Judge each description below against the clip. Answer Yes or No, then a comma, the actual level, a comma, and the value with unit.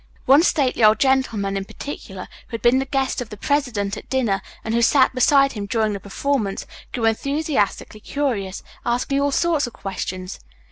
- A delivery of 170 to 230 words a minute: Yes, average, 180 wpm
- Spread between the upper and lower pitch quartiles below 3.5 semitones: No, average, 5.3 semitones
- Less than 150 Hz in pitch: No, high, 240 Hz